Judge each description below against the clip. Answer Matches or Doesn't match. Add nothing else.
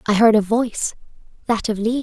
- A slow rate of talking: Doesn't match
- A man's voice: Doesn't match